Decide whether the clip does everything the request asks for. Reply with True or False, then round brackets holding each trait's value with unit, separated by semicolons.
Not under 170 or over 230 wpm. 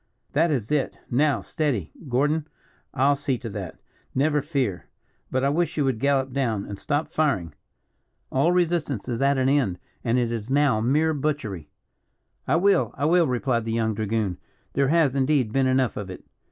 True (180 wpm)